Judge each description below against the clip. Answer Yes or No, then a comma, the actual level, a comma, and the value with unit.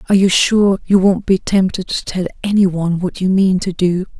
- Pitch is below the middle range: No, medium, 185 Hz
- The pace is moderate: No, fast, 230 wpm